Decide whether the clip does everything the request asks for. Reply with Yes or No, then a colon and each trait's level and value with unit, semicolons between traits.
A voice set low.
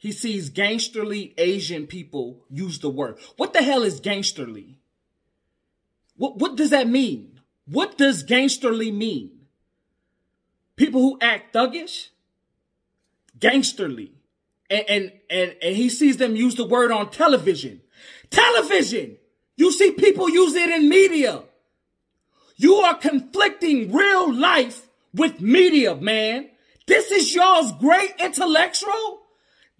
No: very high, 255 Hz